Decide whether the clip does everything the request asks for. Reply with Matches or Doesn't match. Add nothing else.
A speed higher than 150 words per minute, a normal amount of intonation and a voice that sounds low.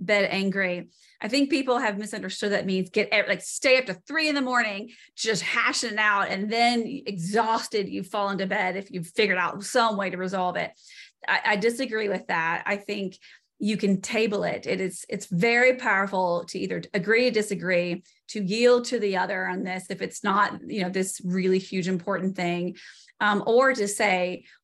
Doesn't match